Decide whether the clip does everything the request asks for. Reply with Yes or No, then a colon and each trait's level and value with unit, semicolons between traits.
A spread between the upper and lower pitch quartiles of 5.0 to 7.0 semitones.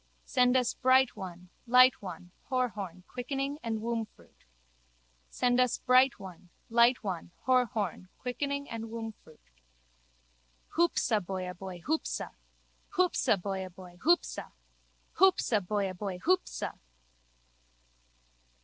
Yes: wide, 5.4 semitones